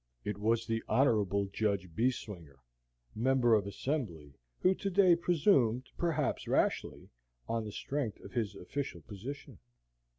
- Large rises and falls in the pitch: Yes, wide, 5.7 semitones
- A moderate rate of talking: No, slow, 130 wpm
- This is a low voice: Yes, low, 115 Hz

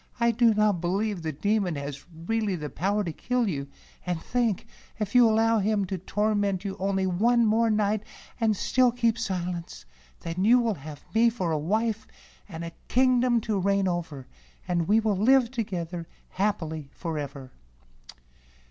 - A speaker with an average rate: Yes, average, 165 wpm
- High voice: Yes, high, 200 Hz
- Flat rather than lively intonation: No, average, 4.6 semitones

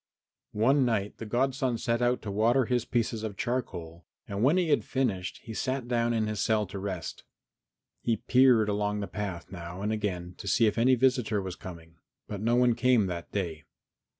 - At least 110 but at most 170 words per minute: No, average, 200 wpm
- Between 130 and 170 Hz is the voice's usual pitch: No, low, 110 Hz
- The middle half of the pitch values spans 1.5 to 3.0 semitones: No, average, 3.8 semitones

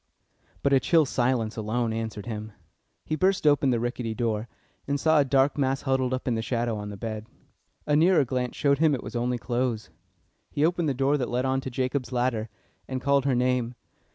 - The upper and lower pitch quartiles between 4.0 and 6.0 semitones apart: No, average, 3.0 semitones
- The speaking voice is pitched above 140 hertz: No, low, 125 Hz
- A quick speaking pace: Yes, fast, 210 wpm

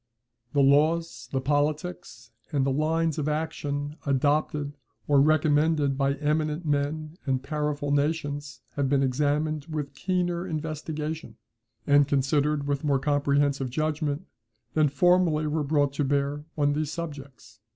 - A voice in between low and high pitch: Yes, medium, 145 Hz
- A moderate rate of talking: No, slow, 130 wpm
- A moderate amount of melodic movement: No, narrow, 1.6 semitones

